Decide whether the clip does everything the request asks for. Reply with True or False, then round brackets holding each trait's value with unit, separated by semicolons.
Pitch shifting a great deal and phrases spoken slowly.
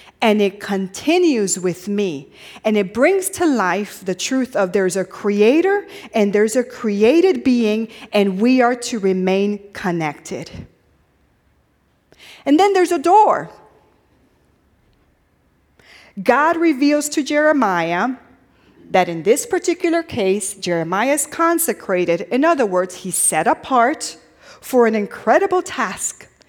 True (7.5 semitones; 120 wpm)